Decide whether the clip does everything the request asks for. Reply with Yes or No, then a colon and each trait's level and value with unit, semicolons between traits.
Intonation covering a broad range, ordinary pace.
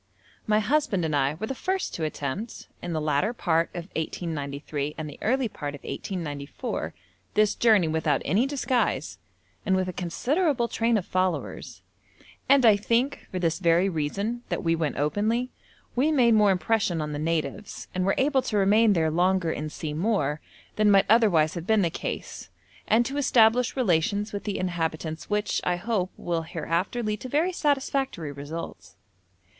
Yes: wide, 6.1 semitones; average, 170 wpm